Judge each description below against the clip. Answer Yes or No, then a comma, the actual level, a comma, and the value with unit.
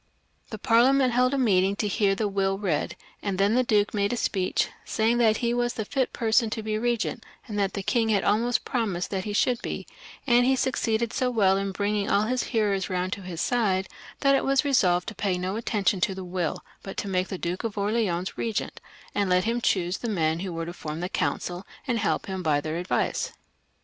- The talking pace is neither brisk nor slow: No, fast, 230 wpm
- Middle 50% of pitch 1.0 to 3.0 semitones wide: No, average, 3.9 semitones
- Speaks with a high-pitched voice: Yes, high, 205 Hz